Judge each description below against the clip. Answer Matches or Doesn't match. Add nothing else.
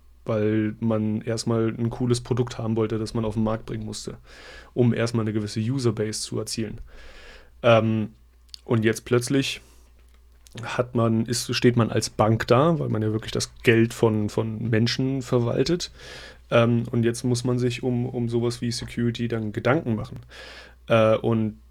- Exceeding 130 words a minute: Matches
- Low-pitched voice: Matches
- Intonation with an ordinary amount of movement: Doesn't match